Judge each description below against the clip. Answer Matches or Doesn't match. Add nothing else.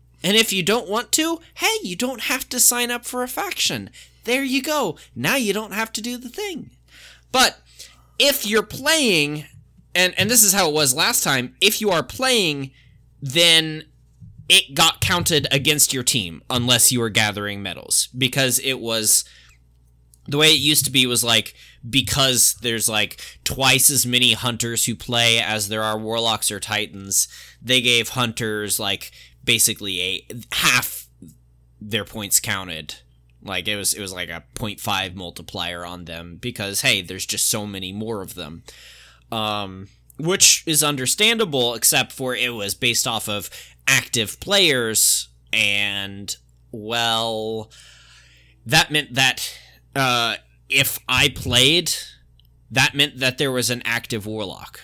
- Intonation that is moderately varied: Doesn't match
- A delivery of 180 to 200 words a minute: Doesn't match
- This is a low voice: Matches